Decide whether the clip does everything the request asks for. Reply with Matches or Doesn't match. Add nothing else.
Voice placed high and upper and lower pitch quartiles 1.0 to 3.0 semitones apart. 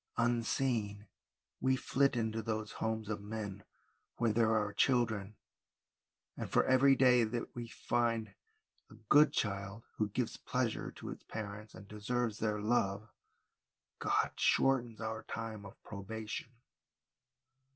Doesn't match